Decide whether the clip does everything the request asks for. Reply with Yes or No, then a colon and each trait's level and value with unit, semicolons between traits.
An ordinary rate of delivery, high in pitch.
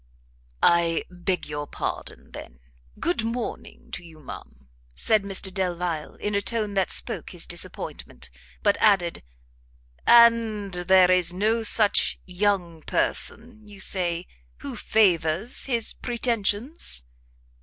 No: slow, 120 wpm; high, 195 Hz